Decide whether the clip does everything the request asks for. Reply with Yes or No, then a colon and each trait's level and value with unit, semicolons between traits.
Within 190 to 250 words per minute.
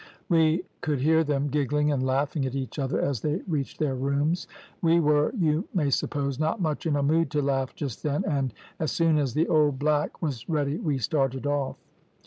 Yes: average, 200 wpm